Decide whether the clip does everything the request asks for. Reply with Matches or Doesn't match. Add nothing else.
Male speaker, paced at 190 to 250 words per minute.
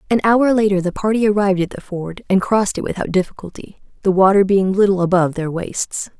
Doesn't match